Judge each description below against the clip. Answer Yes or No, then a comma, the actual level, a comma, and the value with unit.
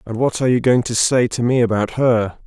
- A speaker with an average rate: No, fast, 270 wpm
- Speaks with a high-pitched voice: No, low, 120 Hz